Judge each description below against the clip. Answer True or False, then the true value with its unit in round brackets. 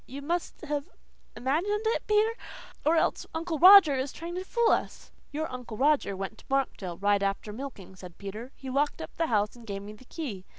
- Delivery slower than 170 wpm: False (205 wpm)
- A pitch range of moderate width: False (7.9 semitones)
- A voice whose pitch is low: False (270 Hz)